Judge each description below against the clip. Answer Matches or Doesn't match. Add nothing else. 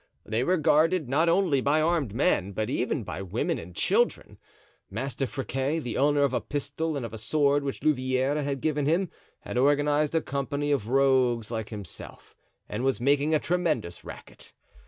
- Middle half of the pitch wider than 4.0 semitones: Doesn't match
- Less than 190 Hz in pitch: Matches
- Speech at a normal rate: Matches